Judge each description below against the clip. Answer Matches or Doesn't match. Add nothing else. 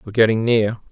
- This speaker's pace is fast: Doesn't match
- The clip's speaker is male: Matches